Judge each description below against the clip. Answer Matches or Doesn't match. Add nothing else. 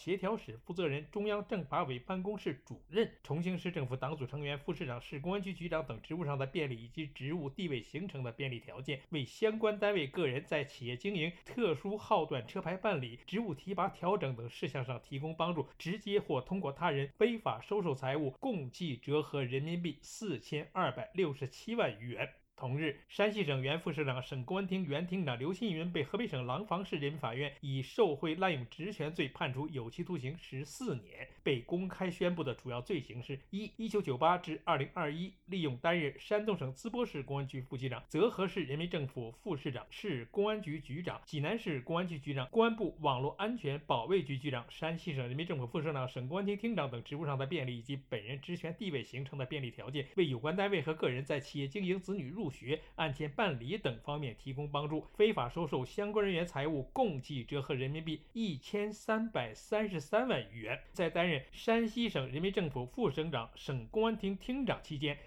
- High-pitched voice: Doesn't match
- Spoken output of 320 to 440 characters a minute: Matches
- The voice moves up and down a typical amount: Doesn't match